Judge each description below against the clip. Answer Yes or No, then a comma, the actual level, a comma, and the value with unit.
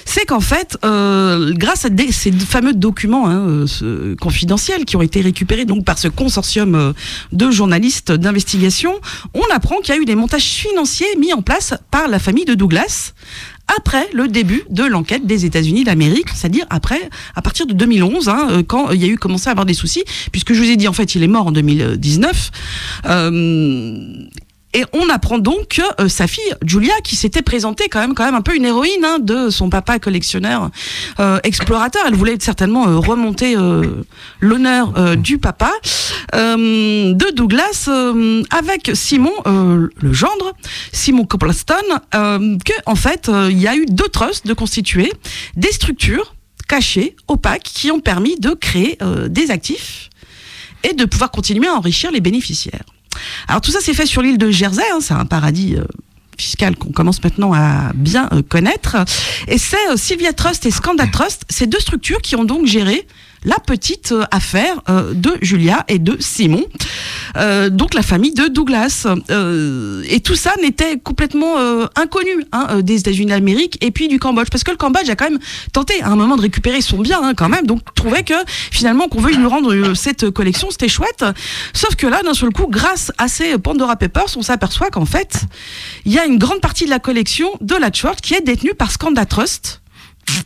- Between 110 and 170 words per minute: No, average, 195 wpm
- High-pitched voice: Yes, high, 225 Hz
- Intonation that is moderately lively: No, wide, 6.6 semitones